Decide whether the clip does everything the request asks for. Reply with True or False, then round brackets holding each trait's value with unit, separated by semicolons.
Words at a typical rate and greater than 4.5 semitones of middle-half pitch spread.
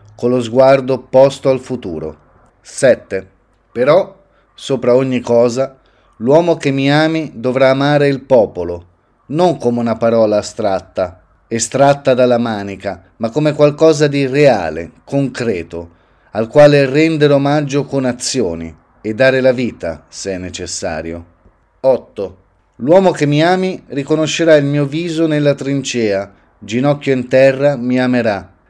True (130 wpm; 5.4 semitones)